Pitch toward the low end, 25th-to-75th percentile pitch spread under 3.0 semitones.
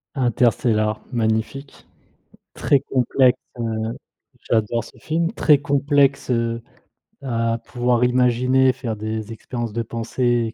Yes: low, 120 Hz; narrow, 2.4 semitones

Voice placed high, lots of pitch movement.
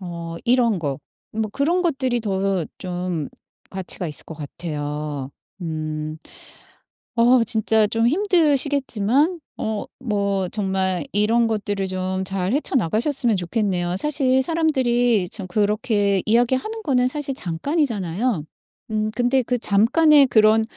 Yes: high, 215 Hz; wide, 5.7 semitones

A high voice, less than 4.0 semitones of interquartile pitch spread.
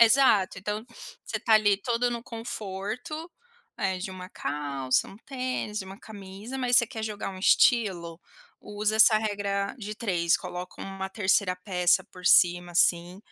Yes: high, 200 Hz; average, 3.3 semitones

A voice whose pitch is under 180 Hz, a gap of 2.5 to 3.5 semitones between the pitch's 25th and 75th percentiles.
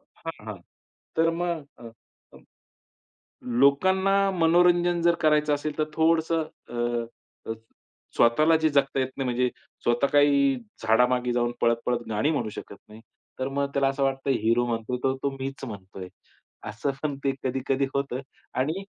No: low, 135 Hz; average, 4.3 semitones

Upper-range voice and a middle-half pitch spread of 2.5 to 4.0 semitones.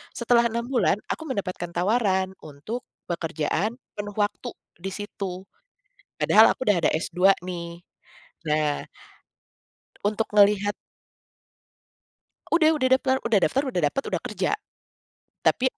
No: high, 205 Hz; average, 5.1 semitones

